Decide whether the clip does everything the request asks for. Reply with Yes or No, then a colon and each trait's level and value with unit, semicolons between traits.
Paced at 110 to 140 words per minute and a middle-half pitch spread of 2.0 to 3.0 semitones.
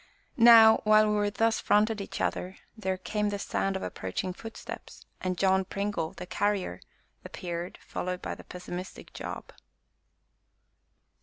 Yes: slow, 135 wpm; narrow, 2.5 semitones